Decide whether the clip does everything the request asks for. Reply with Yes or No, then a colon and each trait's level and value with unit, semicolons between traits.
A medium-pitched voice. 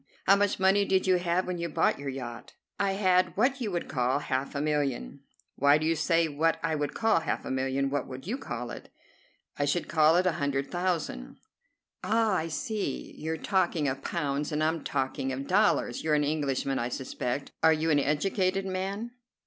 Yes: medium, 155 Hz